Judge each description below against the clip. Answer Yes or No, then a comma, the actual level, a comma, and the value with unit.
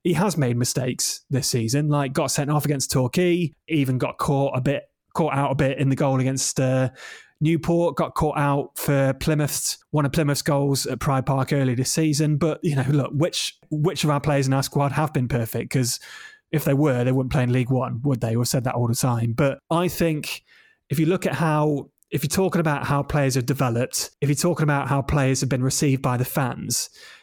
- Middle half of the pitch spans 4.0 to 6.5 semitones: No, average, 2.8 semitones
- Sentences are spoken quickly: Yes, fast, 225 wpm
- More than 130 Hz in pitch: Yes, medium, 140 Hz